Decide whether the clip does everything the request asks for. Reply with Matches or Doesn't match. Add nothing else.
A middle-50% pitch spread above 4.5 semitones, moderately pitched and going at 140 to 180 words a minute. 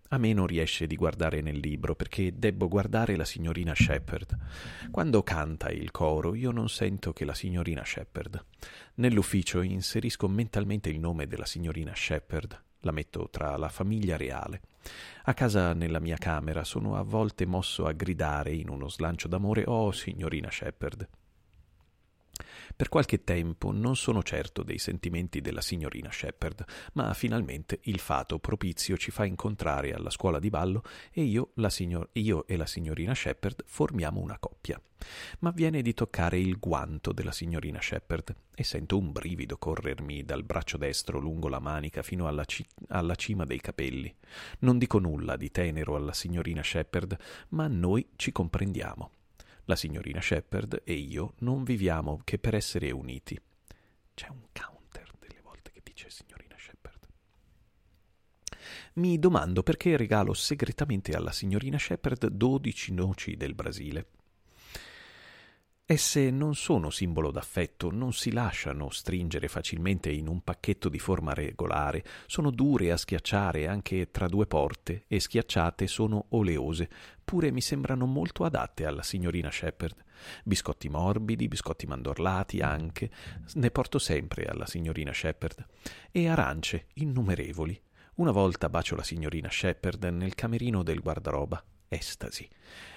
Doesn't match